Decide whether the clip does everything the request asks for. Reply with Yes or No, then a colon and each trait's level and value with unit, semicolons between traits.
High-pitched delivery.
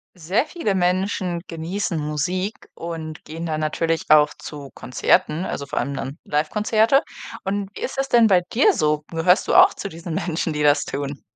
No: medium, 165 Hz